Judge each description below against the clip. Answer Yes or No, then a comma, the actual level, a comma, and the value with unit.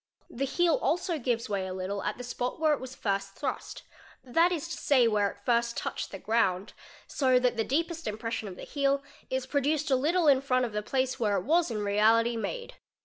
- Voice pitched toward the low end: No, very high, 250 Hz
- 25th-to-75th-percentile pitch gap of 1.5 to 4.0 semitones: No, average, 5.1 semitones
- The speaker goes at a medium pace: No, fast, 215 wpm